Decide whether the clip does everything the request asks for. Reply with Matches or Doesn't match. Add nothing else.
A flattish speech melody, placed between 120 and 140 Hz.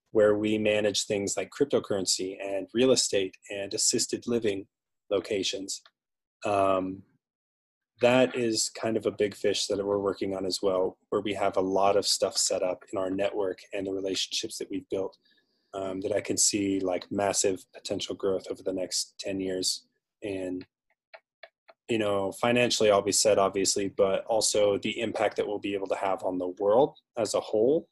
Doesn't match